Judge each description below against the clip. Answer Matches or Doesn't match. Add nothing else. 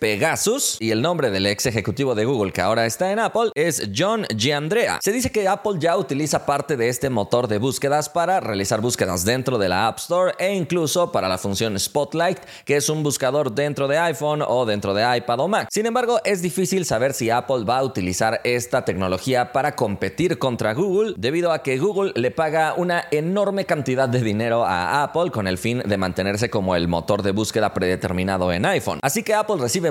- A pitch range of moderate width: Doesn't match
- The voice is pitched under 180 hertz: Matches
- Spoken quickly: Matches